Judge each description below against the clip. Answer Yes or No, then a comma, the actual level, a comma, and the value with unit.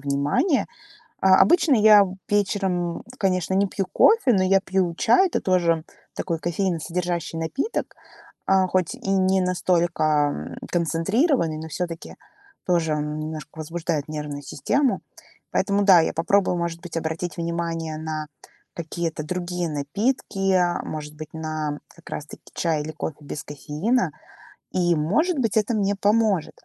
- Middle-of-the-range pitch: Yes, medium, 175 Hz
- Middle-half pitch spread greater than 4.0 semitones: No, average, 3.7 semitones